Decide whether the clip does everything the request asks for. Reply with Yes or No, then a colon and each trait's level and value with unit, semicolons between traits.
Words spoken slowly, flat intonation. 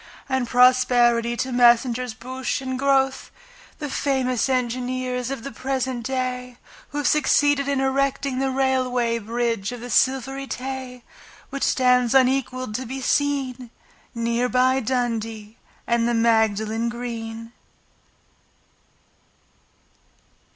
Yes: slow, 115 wpm; narrow, 2.0 semitones